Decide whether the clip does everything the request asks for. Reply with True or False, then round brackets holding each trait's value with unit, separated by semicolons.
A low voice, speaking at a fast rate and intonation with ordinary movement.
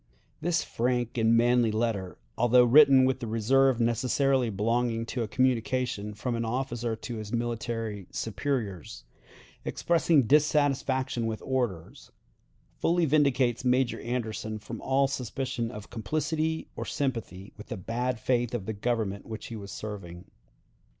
False (120 Hz; 135 wpm; 3.0 semitones)